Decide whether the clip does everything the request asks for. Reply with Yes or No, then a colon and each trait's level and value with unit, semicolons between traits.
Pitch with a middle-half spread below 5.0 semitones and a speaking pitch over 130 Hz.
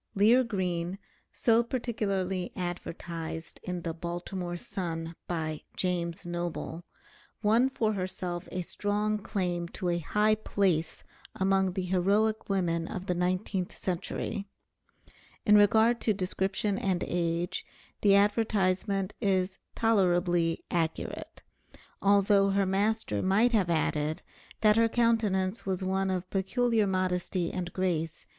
Yes: average, 2.9 semitones; high, 190 Hz